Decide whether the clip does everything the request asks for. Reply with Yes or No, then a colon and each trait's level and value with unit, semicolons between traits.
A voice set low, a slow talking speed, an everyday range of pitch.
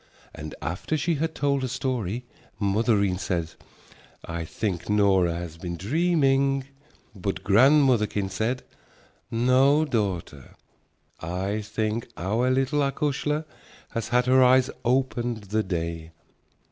No: low, 115 Hz; slow, 115 wpm; wide, 5.9 semitones